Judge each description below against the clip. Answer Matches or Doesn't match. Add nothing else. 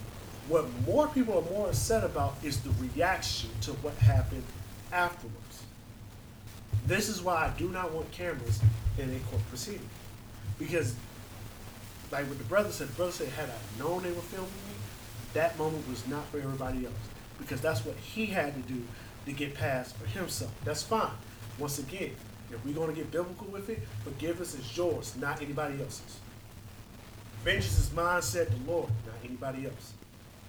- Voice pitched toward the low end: Matches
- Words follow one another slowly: Doesn't match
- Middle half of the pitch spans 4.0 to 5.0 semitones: Doesn't match